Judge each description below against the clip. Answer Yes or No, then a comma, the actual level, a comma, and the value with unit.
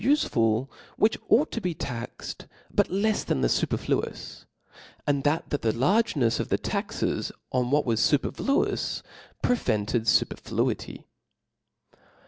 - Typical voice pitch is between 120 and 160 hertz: Yes, medium, 140 Hz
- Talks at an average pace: No, slow, 115 wpm